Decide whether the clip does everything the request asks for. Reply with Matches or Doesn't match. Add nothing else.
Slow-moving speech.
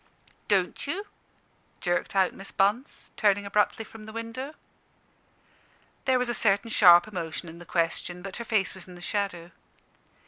Doesn't match